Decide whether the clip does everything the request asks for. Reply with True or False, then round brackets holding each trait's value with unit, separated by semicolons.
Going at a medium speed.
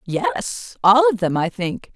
True (185 wpm)